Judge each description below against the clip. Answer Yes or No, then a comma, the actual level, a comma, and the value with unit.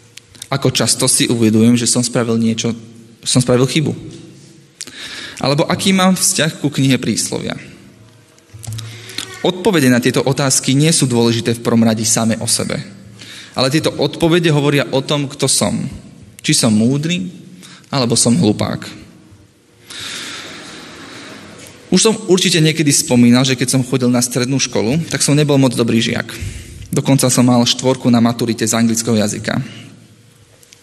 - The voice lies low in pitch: Yes, low, 125 Hz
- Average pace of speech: Yes, average, 140 wpm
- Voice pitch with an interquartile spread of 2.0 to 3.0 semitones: No, average, 3.9 semitones